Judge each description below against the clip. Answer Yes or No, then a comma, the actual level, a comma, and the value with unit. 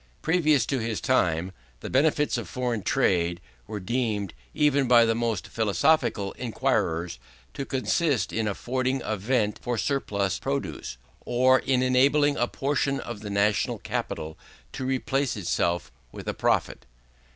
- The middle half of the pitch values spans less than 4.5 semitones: No, average, 4.8 semitones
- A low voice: Yes, low, 120 Hz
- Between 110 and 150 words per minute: Yes, average, 140 wpm